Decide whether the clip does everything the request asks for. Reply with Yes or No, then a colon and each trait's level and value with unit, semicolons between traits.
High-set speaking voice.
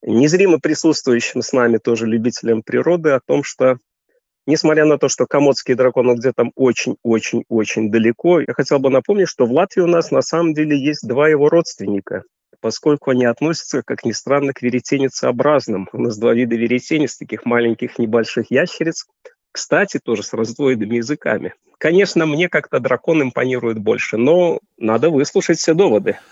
No: low, 135 Hz